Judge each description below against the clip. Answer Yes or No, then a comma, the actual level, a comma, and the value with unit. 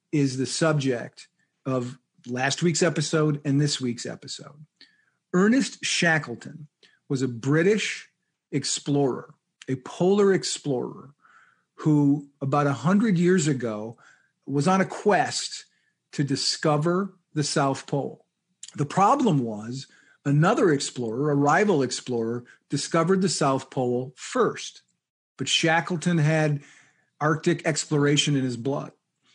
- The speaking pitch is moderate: Yes, medium, 145 Hz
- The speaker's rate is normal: No, slow, 110 wpm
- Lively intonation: No, average, 3.9 semitones